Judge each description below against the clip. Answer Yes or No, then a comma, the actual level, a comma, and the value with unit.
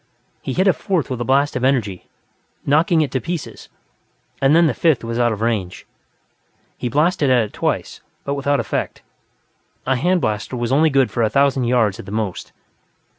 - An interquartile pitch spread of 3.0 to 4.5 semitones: Yes, average, 4.1 semitones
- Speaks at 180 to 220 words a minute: Yes, average, 190 wpm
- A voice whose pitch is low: Yes, low, 130 Hz